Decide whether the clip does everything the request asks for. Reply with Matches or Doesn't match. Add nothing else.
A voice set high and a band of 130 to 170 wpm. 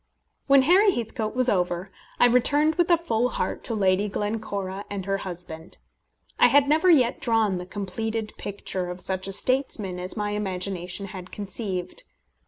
Matches